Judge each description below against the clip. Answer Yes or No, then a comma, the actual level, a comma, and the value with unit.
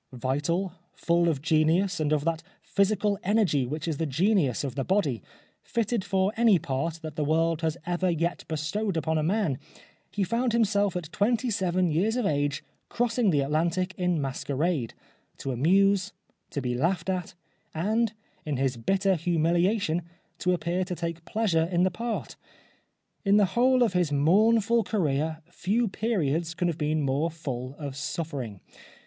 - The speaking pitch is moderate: Yes, medium, 170 Hz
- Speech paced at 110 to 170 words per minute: Yes, average, 165 wpm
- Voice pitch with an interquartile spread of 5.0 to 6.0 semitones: No, average, 4.6 semitones